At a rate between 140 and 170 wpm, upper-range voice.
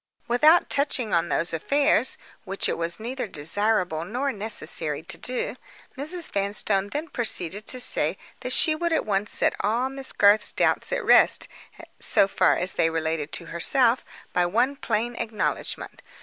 Yes: average, 160 wpm; high, 215 Hz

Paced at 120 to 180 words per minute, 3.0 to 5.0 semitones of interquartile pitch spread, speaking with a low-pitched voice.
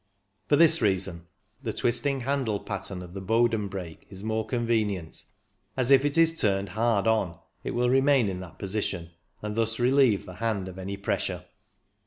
Yes: average, 175 wpm; average, 4.2 semitones; low, 110 Hz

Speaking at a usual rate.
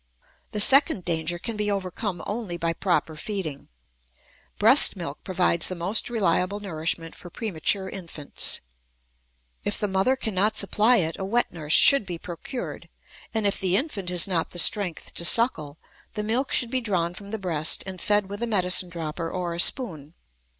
Yes: average, 170 wpm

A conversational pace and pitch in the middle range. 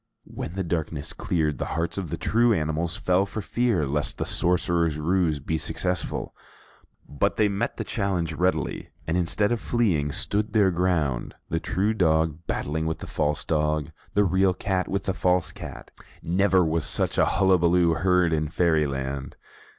No: average, 165 wpm; very low, 85 Hz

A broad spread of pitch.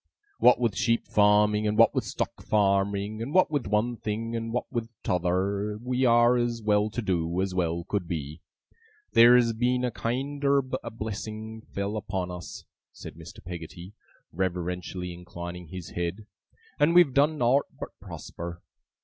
No: average, 4.7 semitones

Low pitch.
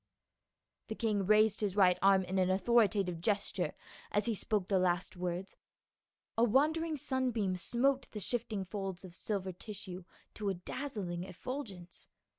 No: high, 200 Hz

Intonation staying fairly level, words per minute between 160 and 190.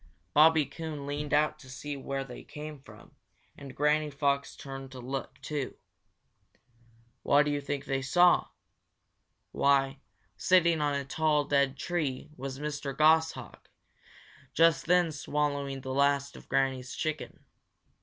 No: narrow, 2.0 semitones; slow, 135 wpm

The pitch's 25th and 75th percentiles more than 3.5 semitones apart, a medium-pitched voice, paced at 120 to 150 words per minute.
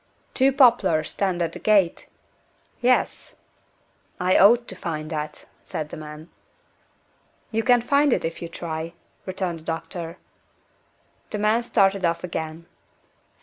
Yes: average, 5.1 semitones; medium, 180 Hz; slow, 135 wpm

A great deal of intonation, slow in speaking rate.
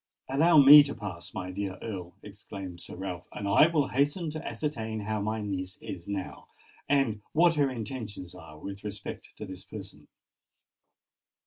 No: wide, 6.6 semitones; average, 160 wpm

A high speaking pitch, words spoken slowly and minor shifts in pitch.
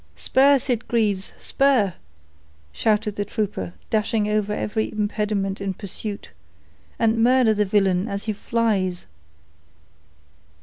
Yes: high, 210 Hz; slow, 100 wpm; narrow, 2.2 semitones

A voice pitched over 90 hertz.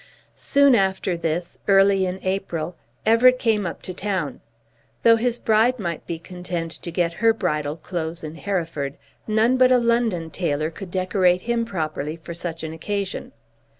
Yes: medium, 185 Hz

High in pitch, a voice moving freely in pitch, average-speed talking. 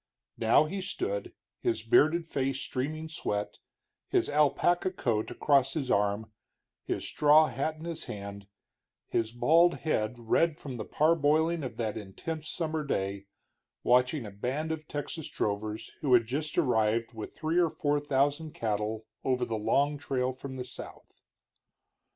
No: low, 135 Hz; wide, 5.8 semitones; average, 150 wpm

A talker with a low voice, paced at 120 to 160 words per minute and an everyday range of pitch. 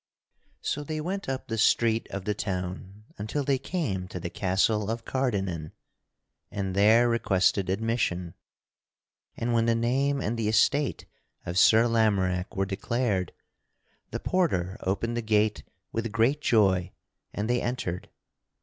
Yes: low, 110 Hz; average, 140 wpm; average, 3.9 semitones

